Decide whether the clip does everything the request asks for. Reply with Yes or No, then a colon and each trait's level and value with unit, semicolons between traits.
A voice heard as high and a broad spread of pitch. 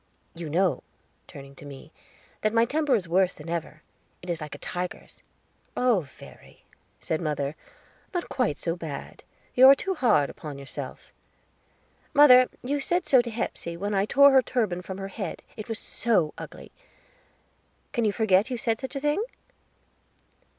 Yes: high, 205 Hz; wide, 7.1 semitones